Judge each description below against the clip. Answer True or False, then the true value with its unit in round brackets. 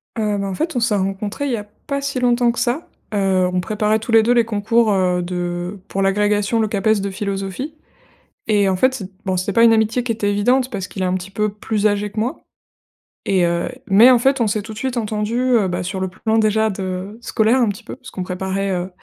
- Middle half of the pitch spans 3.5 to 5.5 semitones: False (3.1 semitones)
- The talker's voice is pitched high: True (210 Hz)